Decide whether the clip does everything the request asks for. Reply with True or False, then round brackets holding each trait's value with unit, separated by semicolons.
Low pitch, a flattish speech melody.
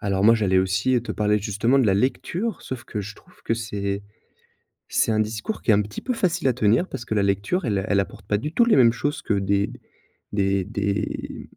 False (105 Hz; 3.7 semitones)